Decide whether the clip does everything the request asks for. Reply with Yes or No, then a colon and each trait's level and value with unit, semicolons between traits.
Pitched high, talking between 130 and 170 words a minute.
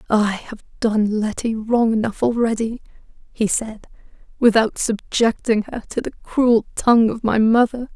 Yes: high, 225 Hz; average, 145 wpm